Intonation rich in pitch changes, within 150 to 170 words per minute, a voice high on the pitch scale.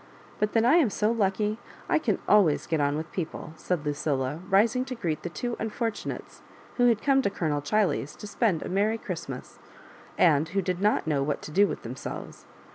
No: wide, 6.1 semitones; average, 200 wpm; high, 195 Hz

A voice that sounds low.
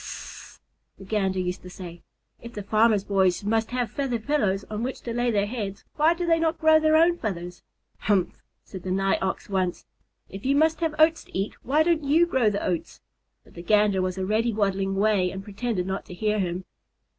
No: high, 210 Hz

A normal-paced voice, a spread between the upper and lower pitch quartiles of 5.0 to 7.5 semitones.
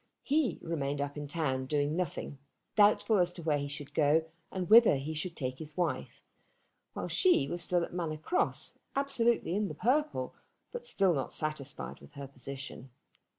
Yes: average, 175 wpm; wide, 5.6 semitones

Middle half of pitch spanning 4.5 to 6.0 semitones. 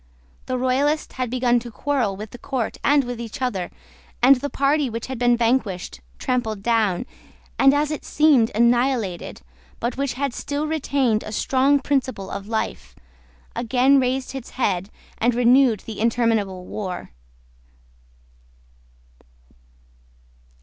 No: average, 3.5 semitones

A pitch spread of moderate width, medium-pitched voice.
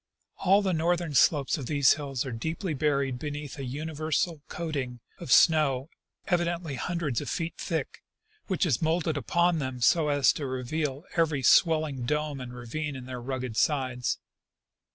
Yes: average, 3.7 semitones; medium, 150 Hz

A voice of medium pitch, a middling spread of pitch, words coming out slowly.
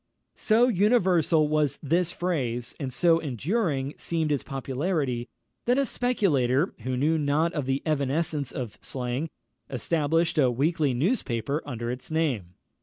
Yes: medium, 150 Hz; average, 4.5 semitones; slow, 130 wpm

